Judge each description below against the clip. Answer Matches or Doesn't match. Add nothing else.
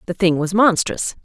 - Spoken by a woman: Matches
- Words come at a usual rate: Matches